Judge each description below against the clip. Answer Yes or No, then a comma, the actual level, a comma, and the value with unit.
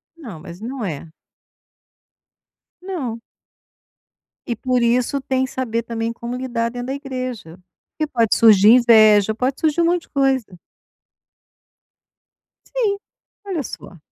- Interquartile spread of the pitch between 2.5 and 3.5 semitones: Yes, average, 3.2 semitones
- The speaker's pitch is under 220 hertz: No, high, 245 Hz